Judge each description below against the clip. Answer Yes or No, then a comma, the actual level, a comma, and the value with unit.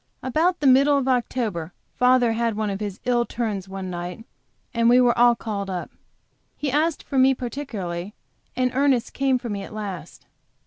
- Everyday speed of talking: Yes, average, 180 wpm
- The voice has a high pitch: Yes, high, 235 Hz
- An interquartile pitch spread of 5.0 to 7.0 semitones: No, average, 4.3 semitones